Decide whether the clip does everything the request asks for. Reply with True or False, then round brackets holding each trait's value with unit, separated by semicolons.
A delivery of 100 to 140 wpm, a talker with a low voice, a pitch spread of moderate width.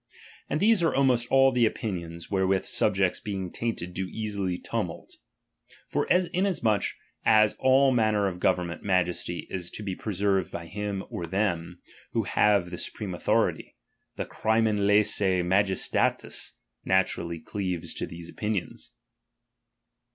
True (135 wpm; 100 Hz; 3.5 semitones)